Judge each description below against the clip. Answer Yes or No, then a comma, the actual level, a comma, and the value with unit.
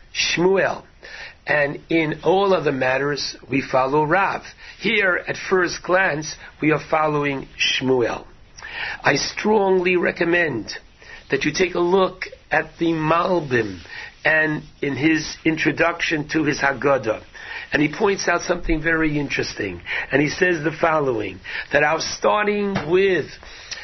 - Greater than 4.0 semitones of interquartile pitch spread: No, average, 3.5 semitones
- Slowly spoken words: Yes, slow, 130 wpm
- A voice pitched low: No, medium, 160 Hz